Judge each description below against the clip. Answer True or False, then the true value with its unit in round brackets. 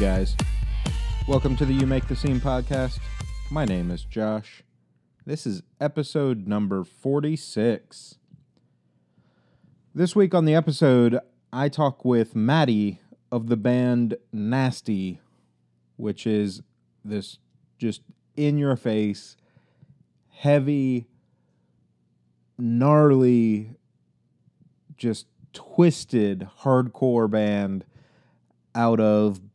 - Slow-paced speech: True (95 wpm)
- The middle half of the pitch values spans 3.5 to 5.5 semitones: True (5.2 semitones)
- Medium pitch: False (115 Hz)